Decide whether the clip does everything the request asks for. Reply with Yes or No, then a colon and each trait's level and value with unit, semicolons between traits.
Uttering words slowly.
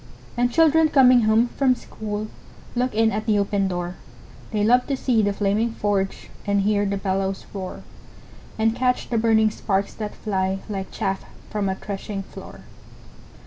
No: average, 165 wpm